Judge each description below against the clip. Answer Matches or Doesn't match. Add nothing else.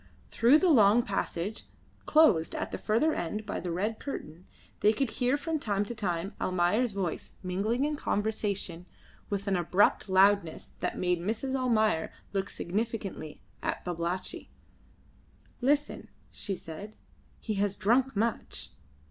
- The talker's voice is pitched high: Matches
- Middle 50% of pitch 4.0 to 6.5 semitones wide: Matches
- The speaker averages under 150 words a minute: Matches